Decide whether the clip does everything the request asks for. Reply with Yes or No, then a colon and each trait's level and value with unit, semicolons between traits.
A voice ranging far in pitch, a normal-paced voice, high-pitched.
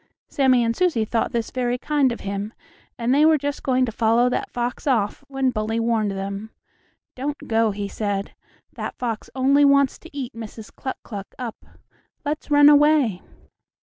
No: average, 4.1 semitones; average, 175 wpm; high, 245 Hz